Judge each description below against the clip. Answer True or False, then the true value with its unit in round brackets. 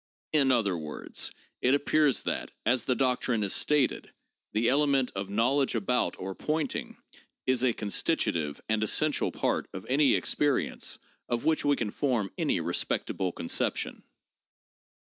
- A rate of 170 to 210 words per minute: False (145 wpm)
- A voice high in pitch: False (125 Hz)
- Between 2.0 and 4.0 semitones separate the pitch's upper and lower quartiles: False (5.2 semitones)